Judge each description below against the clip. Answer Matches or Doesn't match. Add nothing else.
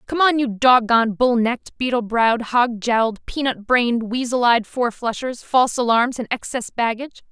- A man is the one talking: Doesn't match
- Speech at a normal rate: Doesn't match